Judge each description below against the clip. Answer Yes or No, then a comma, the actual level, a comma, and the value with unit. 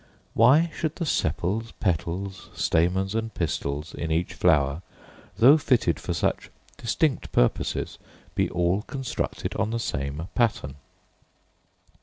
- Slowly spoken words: Yes, slow, 120 wpm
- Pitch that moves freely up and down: Yes, wide, 6.1 semitones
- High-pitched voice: No, very low, 95 Hz